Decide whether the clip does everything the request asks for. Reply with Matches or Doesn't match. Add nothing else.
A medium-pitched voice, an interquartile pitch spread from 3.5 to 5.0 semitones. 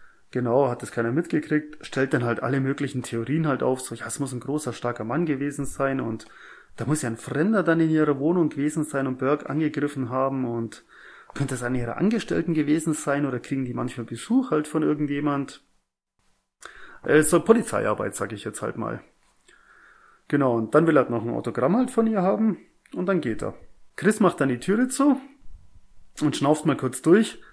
Matches